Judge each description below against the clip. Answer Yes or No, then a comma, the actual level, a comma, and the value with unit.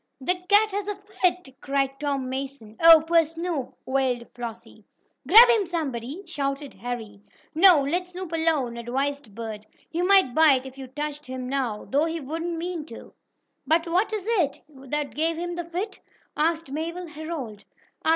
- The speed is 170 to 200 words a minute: No, average, 160 wpm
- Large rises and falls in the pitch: No, average, 4.7 semitones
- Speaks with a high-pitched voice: Yes, very high, 300 Hz